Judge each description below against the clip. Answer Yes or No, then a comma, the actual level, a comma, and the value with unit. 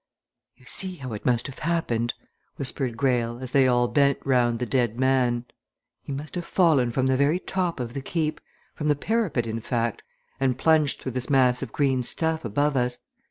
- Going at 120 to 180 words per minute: No, average, 195 wpm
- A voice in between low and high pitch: No, low, 130 Hz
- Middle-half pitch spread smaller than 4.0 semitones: Yes, average, 3.4 semitones